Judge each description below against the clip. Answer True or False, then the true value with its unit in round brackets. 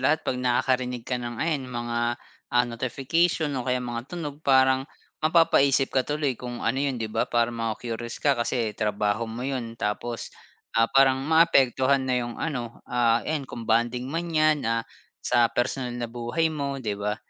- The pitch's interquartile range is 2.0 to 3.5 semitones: True (2.8 semitones)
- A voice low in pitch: True (125 Hz)